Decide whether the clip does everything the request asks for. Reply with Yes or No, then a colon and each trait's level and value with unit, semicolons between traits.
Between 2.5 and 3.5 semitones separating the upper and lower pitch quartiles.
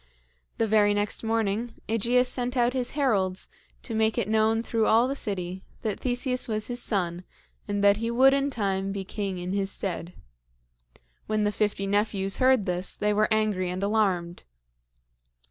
Yes: average, 3.0 semitones